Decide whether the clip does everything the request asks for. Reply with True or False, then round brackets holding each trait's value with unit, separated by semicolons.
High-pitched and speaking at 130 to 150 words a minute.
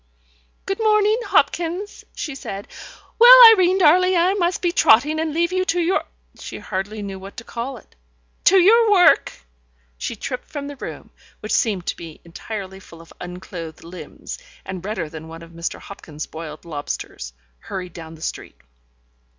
False (225 Hz; 170 wpm)